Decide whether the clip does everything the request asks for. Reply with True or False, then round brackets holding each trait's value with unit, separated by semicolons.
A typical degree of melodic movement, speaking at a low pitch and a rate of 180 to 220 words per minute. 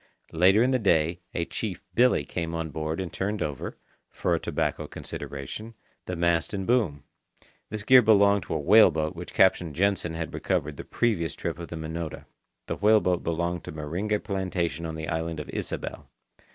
True (4.0 semitones; 85 Hz; 185 wpm)